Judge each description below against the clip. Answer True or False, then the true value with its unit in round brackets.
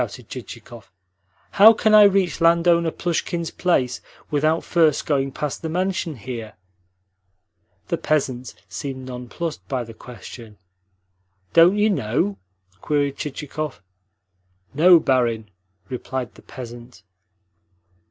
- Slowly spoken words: True (110 wpm)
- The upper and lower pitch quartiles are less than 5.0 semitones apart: False (5.4 semitones)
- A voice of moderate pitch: True (145 Hz)